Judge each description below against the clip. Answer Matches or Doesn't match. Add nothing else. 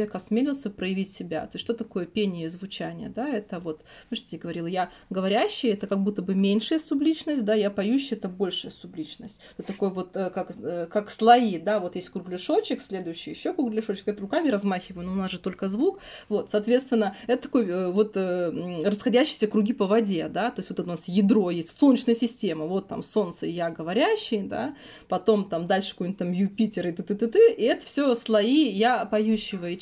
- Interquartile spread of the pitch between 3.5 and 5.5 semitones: Matches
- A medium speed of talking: Doesn't match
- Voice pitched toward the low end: Doesn't match